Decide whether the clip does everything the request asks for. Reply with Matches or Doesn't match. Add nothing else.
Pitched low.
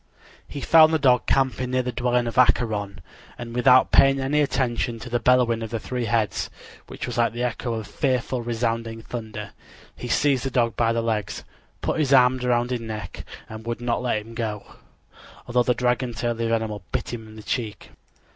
Matches